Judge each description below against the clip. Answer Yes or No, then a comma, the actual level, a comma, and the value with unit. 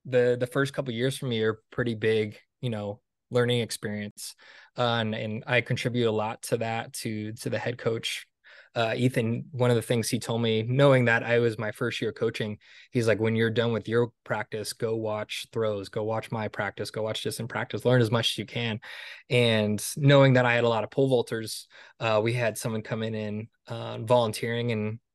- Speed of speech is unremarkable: No, fast, 220 wpm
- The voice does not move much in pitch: Yes, narrow, 2.0 semitones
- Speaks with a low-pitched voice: Yes, low, 115 Hz